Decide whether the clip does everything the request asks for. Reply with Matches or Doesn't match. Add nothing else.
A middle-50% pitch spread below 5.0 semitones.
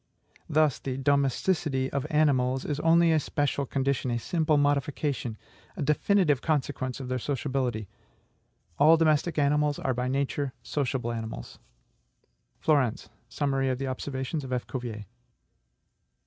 Matches